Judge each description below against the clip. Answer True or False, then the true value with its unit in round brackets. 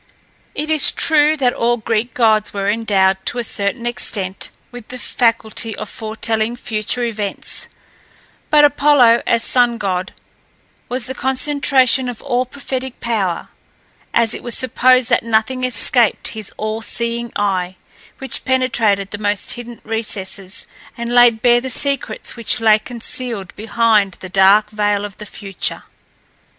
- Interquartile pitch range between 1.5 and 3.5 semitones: True (3.0 semitones)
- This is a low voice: False (230 Hz)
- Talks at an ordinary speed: True (145 wpm)